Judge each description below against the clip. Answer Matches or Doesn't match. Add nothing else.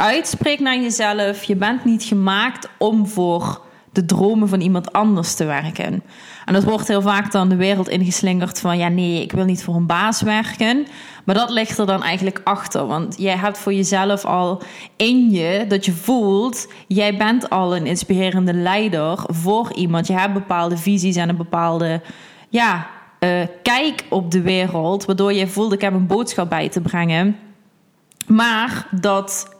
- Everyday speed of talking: Matches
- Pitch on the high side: Matches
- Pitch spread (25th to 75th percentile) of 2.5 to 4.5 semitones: Matches